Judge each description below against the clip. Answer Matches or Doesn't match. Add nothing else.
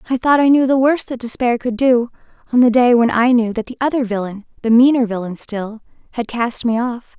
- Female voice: Matches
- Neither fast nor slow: Doesn't match